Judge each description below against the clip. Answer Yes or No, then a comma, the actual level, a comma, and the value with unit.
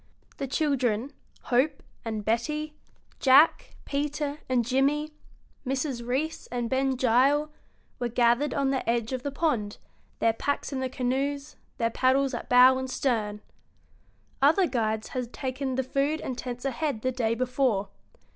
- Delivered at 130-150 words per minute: Yes, average, 145 wpm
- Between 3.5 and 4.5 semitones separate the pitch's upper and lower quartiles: No, average, 2.8 semitones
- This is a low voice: No, very high, 260 Hz